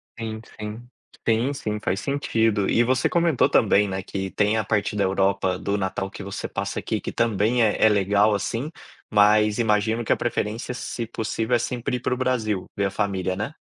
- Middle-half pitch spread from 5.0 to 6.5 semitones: No, average, 2.7 semitones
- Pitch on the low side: Yes, low, 105 Hz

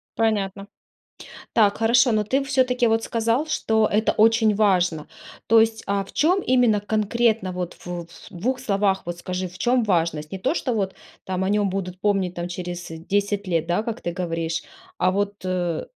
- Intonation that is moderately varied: Yes, average, 3.7 semitones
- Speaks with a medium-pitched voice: No, high, 205 Hz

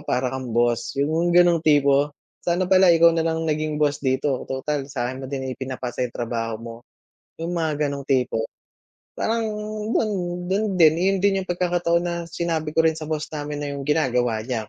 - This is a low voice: No, medium, 150 Hz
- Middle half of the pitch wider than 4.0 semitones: Yes, average, 4.6 semitones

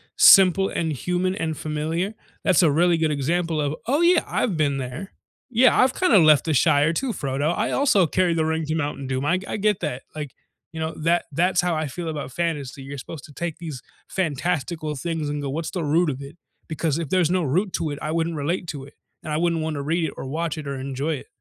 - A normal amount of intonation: Yes, average, 3.3 semitones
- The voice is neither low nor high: Yes, medium, 160 Hz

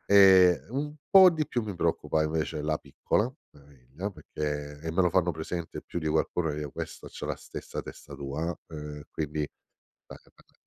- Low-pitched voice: Yes, very low, 80 Hz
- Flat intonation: No, average, 4.0 semitones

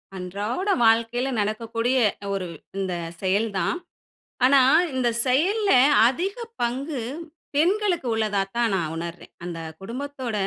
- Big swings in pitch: Yes, wide, 5.8 semitones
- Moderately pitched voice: No, high, 235 Hz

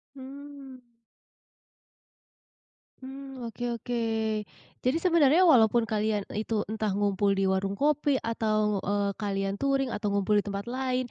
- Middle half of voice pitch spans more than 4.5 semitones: Yes, average, 4.9 semitones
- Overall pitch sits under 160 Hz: No, high, 225 Hz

